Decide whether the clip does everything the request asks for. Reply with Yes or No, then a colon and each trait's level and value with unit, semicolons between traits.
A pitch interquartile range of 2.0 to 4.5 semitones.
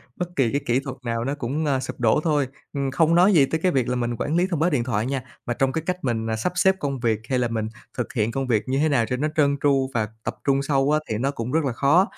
Yes: average, 3.9 semitones